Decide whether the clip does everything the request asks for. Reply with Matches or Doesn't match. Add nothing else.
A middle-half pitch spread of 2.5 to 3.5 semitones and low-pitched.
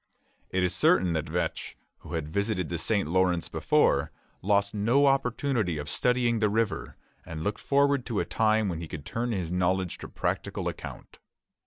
Doesn't match